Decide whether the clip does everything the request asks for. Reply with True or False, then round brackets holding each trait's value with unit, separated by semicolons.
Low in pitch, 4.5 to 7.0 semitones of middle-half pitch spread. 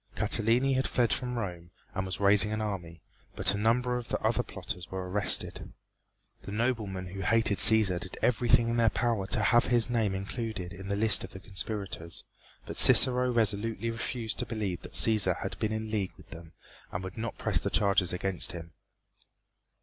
False (105 Hz; 3.5 semitones)